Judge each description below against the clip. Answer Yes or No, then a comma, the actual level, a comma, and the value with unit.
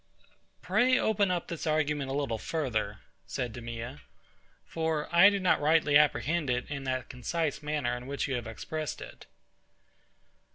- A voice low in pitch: No, medium, 145 Hz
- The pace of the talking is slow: No, average, 155 wpm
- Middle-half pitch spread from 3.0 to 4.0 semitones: No, average, 4.6 semitones